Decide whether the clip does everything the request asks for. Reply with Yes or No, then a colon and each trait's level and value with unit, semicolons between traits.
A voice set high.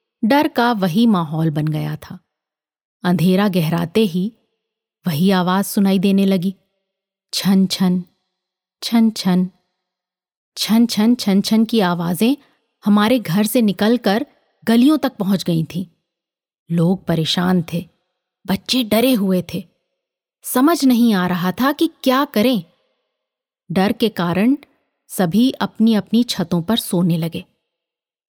Yes: high, 195 Hz